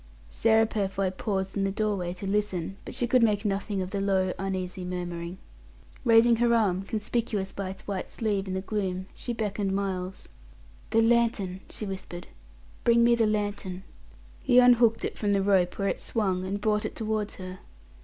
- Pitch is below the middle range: No, high, 200 Hz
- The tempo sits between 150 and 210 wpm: Yes, average, 180 wpm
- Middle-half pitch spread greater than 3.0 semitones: No, average, 2.7 semitones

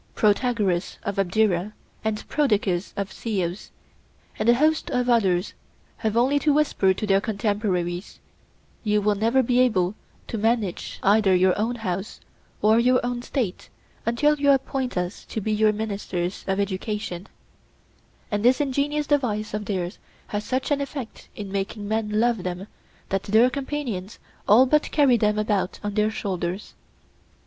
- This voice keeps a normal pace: Yes, average, 150 wpm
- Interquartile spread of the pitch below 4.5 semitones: Yes, average, 4.0 semitones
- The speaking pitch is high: Yes, high, 215 Hz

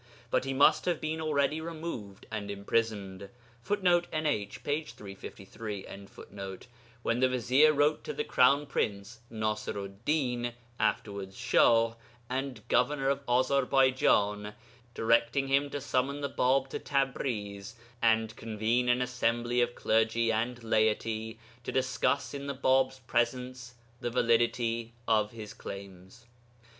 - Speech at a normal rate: No, slow, 125 wpm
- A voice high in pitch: No, low, 120 Hz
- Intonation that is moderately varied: Yes, average, 3.8 semitones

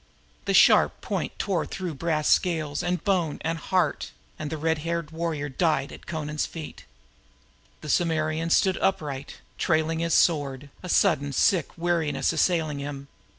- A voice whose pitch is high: No, medium, 160 Hz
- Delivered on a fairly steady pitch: Yes, narrow, 2.2 semitones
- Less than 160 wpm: Yes, average, 145 wpm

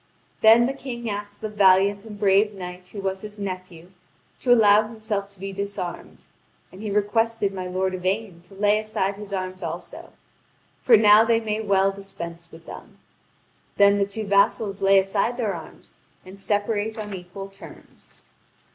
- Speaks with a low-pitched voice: No, high, 200 Hz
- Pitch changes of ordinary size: No, narrow, 2.0 semitones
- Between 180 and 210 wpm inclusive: No, average, 165 wpm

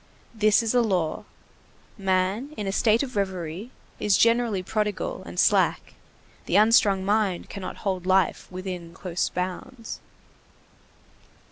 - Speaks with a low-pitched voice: No, high, 200 Hz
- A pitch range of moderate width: Yes, average, 3.1 semitones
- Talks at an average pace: No, slow, 125 wpm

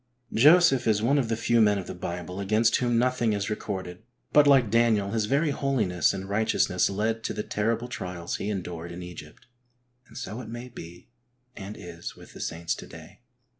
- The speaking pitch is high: No, low, 105 Hz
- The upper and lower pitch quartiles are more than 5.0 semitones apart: No, average, 4.6 semitones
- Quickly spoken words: Yes, fast, 215 wpm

